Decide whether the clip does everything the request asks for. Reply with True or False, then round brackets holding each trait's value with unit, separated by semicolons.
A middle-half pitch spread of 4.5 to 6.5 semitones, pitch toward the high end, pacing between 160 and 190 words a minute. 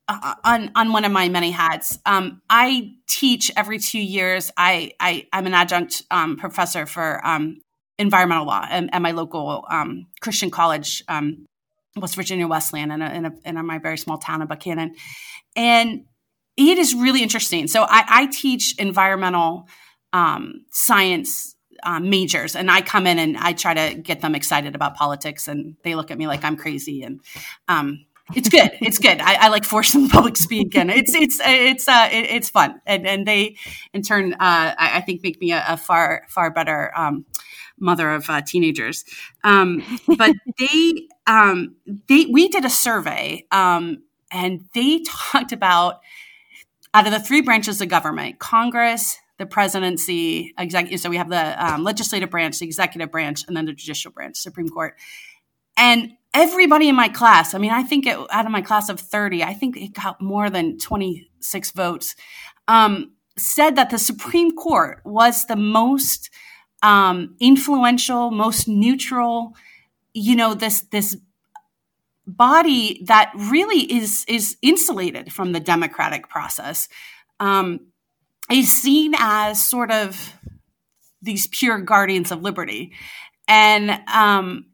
True (5.5 semitones; 205 Hz; 165 wpm)